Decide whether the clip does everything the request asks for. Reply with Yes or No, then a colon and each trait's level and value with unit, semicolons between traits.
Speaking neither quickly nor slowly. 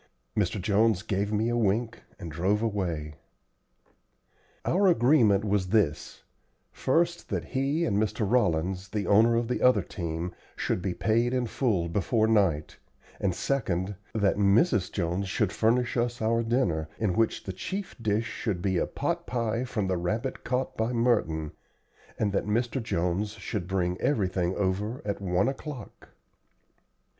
Yes: average, 150 wpm